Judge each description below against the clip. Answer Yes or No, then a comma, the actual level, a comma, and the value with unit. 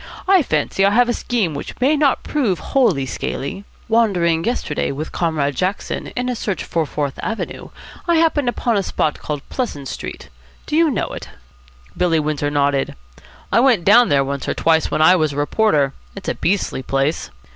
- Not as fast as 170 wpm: No, average, 185 wpm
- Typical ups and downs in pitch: No, wide, 8.6 semitones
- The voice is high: No, medium, 180 Hz